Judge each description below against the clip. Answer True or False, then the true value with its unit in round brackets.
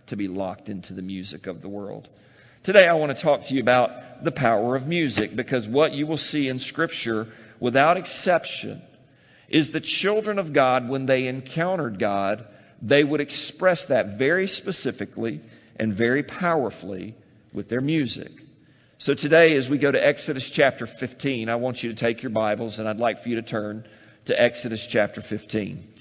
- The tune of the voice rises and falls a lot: False (5.0 semitones)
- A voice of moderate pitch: False (125 Hz)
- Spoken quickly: False (180 wpm)